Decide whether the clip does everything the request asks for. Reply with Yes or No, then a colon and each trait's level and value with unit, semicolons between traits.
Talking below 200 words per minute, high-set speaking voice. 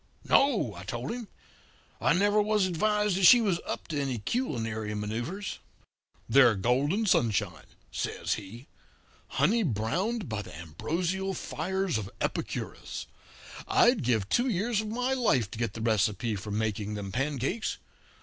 No: average, 145 wpm; medium, 140 Hz